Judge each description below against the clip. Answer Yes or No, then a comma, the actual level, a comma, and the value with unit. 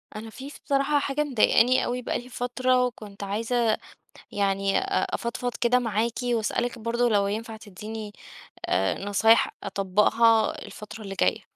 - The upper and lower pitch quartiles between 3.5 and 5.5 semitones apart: No, average, 2.9 semitones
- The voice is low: No, high, 230 Hz